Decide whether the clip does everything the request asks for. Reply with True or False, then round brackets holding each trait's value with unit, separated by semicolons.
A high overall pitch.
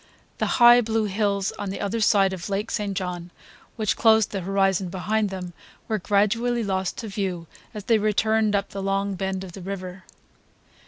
True (200 Hz)